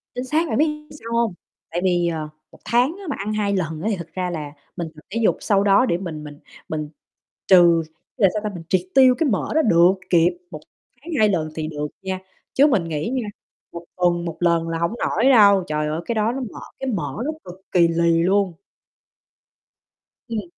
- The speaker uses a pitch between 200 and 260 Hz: No, medium, 185 Hz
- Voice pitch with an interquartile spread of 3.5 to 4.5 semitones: No, average, 5.2 semitones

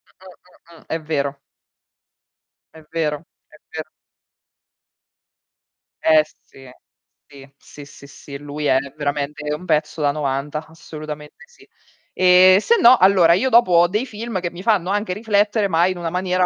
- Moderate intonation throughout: Yes, average, 3.9 semitones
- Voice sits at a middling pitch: Yes, medium, 165 Hz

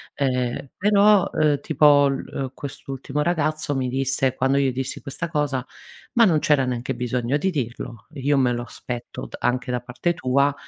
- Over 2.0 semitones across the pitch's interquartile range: Yes, average, 2.8 semitones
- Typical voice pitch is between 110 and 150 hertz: Yes, low, 135 Hz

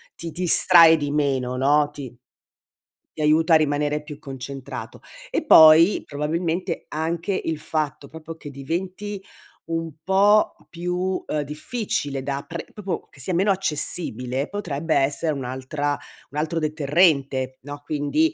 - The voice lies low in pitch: No, medium, 155 Hz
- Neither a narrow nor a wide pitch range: Yes, average, 3.1 semitones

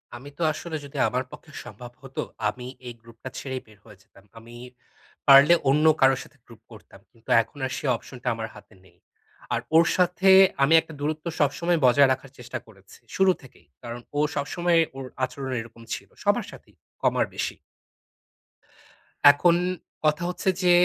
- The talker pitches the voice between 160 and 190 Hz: No, low, 135 Hz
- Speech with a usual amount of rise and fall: Yes, average, 4.8 semitones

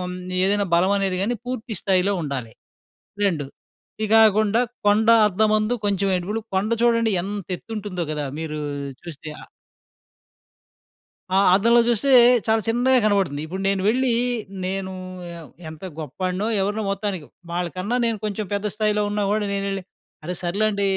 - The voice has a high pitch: Yes, high, 200 Hz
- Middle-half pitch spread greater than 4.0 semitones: No, average, 2.9 semitones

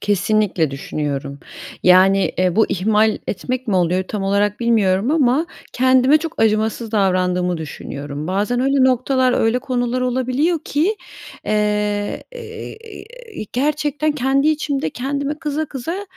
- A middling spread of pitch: No, wide, 6.1 semitones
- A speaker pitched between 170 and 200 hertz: No, high, 235 Hz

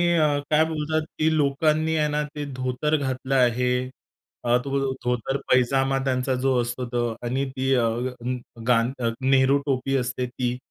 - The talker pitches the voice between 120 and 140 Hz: Yes, low, 135 Hz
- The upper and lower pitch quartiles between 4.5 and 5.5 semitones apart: No, average, 2.9 semitones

